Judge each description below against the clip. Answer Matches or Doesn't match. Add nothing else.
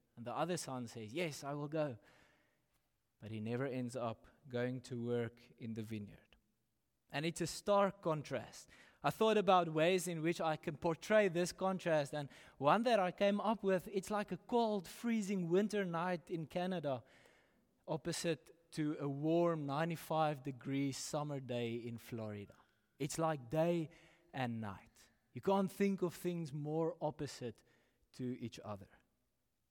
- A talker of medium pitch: Matches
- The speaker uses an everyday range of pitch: Doesn't match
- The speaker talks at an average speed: Matches